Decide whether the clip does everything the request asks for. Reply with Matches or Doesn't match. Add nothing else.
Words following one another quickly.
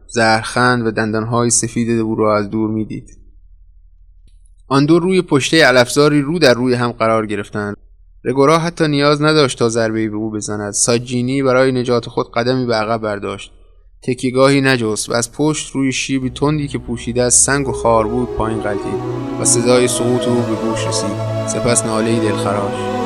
Matches